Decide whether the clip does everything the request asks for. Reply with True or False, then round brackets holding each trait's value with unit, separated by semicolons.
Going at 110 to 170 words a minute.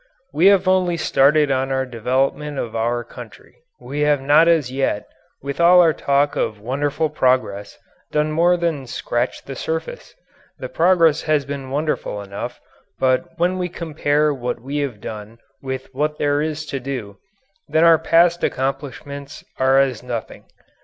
True (160 wpm)